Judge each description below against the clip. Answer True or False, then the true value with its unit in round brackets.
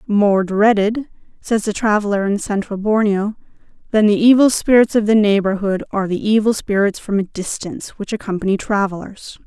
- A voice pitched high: True (205 Hz)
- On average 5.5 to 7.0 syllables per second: False (5.3 syllables/s)